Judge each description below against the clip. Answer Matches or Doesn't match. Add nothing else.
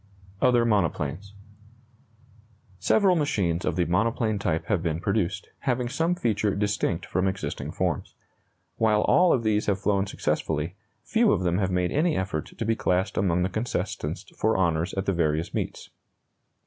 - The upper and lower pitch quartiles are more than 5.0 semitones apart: Doesn't match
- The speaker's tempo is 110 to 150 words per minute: Doesn't match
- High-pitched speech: Doesn't match